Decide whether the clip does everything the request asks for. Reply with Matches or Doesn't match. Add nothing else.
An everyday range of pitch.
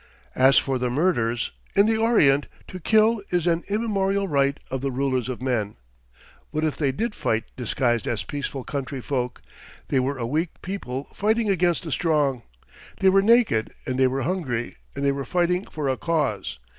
Doesn't match